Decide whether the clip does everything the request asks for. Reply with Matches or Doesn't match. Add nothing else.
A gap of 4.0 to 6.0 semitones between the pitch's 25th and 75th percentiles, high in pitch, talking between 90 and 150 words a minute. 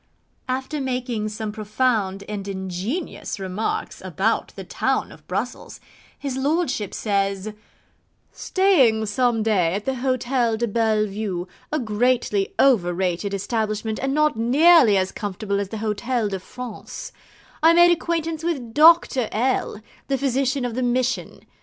Matches